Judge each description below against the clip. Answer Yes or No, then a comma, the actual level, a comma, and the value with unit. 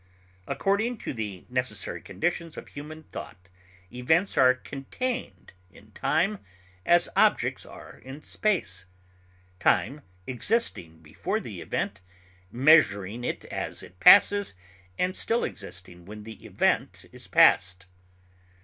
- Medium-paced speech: No, slow, 115 wpm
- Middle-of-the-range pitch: No, low, 130 Hz